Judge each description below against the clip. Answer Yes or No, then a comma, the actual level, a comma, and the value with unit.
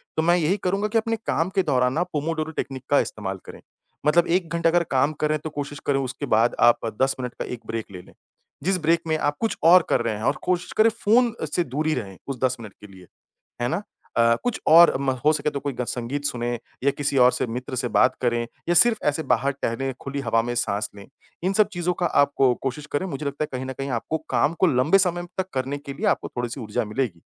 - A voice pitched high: No, medium, 140 Hz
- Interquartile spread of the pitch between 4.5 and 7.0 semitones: Yes, average, 5.2 semitones